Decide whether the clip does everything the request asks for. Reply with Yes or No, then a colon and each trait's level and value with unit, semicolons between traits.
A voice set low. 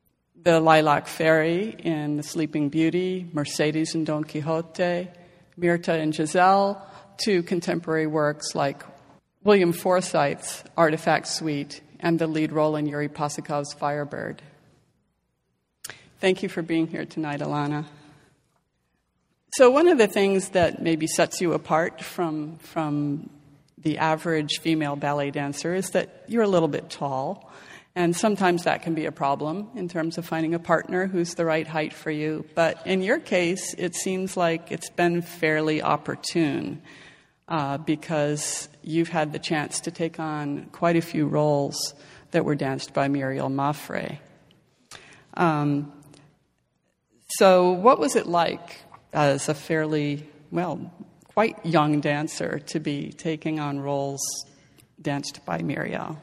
No: medium, 160 Hz